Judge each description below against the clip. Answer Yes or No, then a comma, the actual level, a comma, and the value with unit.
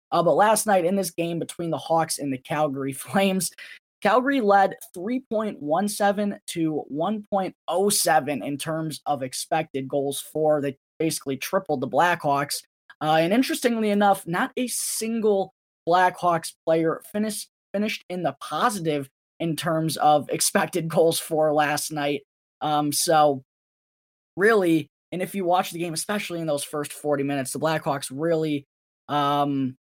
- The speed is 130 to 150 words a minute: Yes, average, 145 wpm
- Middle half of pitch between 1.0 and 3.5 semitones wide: No, average, 5.0 semitones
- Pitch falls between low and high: Yes, medium, 165 Hz